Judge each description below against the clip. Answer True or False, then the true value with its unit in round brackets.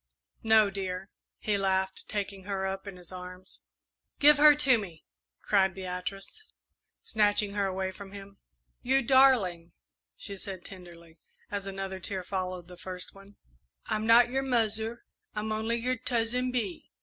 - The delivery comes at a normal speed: True (150 wpm)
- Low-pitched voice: False (200 Hz)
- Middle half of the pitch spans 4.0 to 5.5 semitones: False (3.2 semitones)